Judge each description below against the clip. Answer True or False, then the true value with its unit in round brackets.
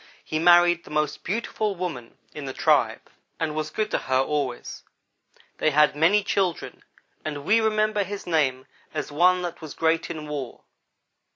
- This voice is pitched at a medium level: True (160 Hz)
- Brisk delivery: False (165 wpm)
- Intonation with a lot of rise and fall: False (3.6 semitones)